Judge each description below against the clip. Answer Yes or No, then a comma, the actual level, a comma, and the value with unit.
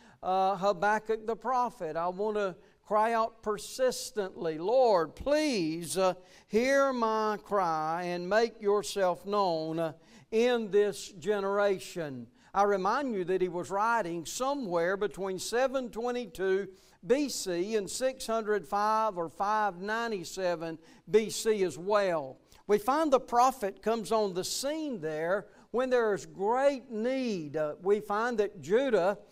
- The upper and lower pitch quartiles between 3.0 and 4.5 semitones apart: Yes, average, 3.6 semitones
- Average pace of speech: No, slow, 125 wpm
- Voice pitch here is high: Yes, high, 205 Hz